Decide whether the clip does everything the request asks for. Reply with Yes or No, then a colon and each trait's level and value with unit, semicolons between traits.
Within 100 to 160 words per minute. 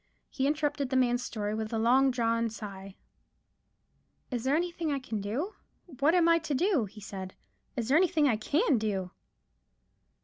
No: average, 170 wpm